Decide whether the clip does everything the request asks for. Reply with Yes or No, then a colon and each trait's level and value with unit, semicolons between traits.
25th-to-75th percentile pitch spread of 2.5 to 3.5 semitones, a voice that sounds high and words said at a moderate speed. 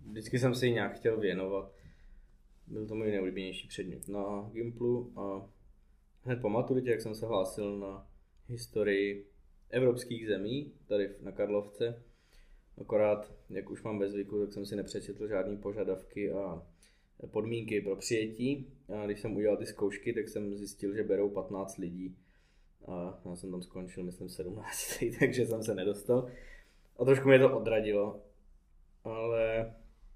No: average, 3.1 semitones; low, 100 Hz; average, 145 wpm